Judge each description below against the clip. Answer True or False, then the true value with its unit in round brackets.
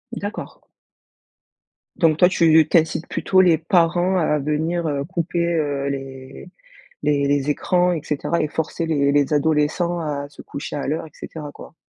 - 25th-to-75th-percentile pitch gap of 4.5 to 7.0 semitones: False (2.8 semitones)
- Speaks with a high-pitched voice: False (155 Hz)